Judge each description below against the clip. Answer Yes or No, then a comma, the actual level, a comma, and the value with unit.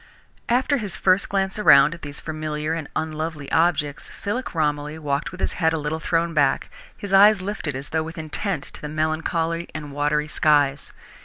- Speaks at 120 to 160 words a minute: No, average, 180 wpm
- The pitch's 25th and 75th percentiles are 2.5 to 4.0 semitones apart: Yes, average, 3.0 semitones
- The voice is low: No, medium, 160 Hz